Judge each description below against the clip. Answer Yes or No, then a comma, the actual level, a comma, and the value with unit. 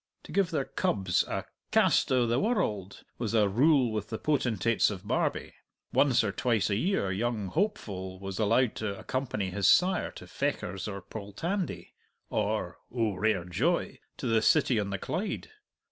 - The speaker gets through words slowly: No, average, 165 wpm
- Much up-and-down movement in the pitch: No, average, 4.9 semitones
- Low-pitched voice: Yes, low, 110 Hz